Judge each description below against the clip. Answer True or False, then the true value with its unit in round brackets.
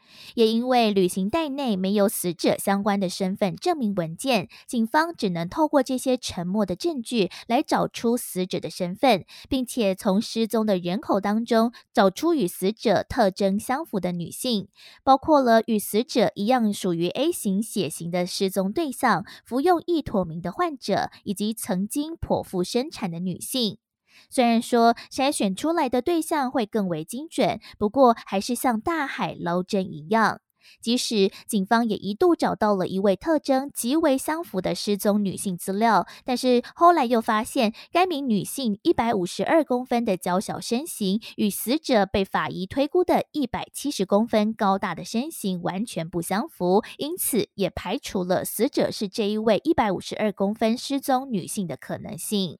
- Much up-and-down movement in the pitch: False (5.0 semitones)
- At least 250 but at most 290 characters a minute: True (260 characters per minute)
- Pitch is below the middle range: False (220 Hz)